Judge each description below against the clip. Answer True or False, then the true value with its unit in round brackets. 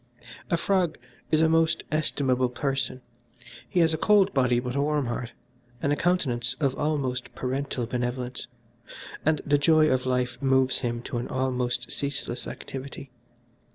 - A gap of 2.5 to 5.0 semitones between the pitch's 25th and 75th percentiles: True (3.6 semitones)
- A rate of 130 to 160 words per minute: True (155 wpm)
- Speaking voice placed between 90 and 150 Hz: True (135 Hz)